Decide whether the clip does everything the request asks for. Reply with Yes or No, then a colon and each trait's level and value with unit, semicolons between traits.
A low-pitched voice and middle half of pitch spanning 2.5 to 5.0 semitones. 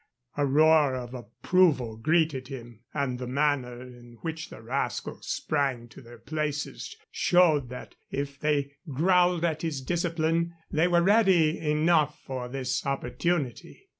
No: medium, 145 Hz; average, 4.4 semitones